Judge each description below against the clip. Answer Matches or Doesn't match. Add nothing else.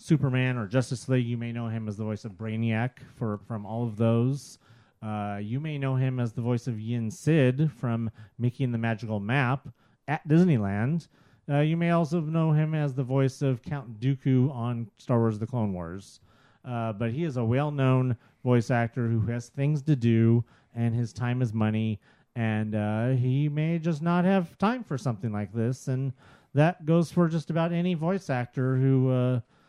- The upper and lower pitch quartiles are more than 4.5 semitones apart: Doesn't match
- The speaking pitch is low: Matches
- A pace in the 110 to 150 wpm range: Doesn't match